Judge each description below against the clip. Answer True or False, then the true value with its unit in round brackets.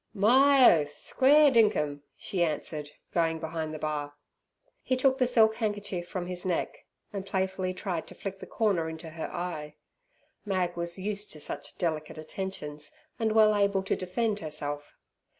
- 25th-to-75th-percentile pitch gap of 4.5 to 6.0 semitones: True (4.9 semitones)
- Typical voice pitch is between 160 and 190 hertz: True (185 Hz)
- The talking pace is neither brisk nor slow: True (160 wpm)